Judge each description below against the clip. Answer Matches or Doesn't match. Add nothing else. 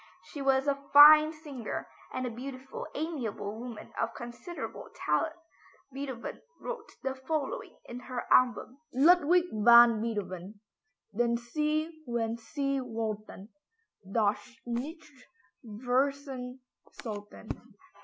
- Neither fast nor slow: Doesn't match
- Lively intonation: Doesn't match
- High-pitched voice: Matches